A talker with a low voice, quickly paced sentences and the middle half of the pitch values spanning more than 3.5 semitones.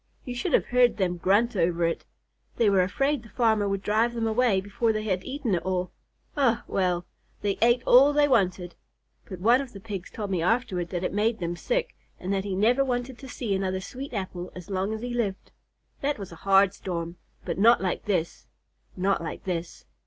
No: high, 200 Hz; fast, 210 wpm; average, 4.6 semitones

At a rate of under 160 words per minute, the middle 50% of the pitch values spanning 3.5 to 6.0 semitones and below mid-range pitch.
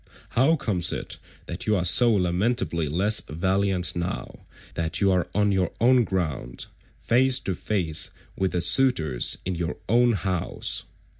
Yes: average, 150 wpm; average, 4.5 semitones; very low, 95 Hz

